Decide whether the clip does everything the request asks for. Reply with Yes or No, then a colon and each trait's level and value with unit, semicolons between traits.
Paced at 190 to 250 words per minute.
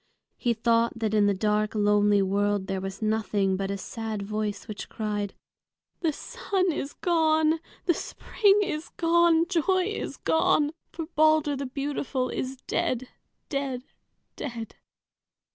No: average, 140 wpm